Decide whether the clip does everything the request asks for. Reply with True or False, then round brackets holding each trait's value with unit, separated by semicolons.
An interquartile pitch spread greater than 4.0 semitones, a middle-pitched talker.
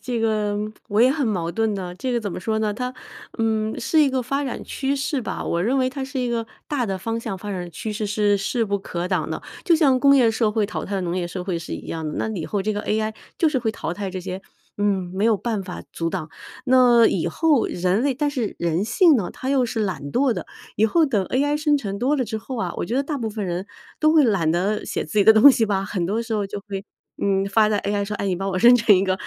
False (4.5 semitones; 215 Hz)